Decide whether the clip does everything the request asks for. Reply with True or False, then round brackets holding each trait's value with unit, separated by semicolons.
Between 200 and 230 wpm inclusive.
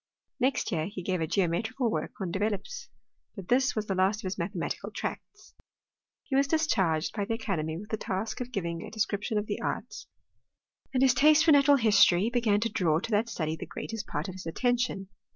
True (205 wpm)